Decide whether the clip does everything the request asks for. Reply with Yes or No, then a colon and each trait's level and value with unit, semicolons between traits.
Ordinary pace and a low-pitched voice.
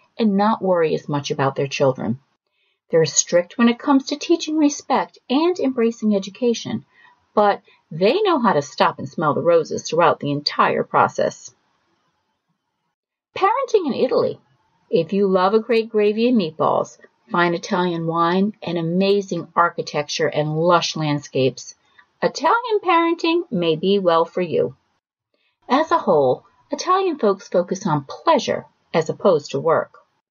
No: average, 145 wpm; high, 200 Hz